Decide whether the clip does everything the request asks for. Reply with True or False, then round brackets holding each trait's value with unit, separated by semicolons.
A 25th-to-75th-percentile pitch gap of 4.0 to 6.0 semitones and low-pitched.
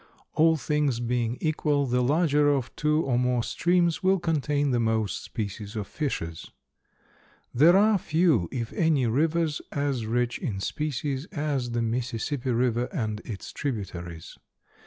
True (4.7 semitones; 130 Hz)